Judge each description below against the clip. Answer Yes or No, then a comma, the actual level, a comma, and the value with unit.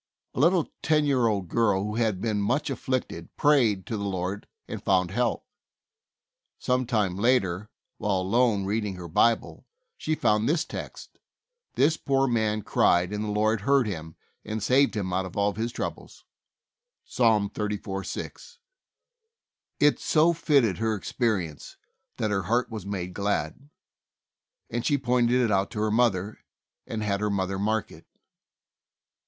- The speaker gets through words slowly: No, average, 155 wpm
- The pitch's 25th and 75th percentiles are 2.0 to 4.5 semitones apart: Yes, average, 4.0 semitones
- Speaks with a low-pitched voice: Yes, low, 110 Hz